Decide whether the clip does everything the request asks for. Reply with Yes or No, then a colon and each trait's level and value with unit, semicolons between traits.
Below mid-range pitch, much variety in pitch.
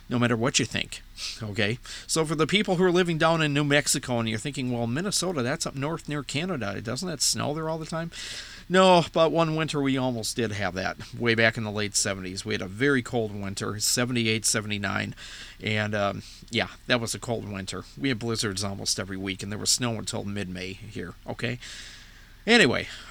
Yes: low, 115 Hz; wide, 5.8 semitones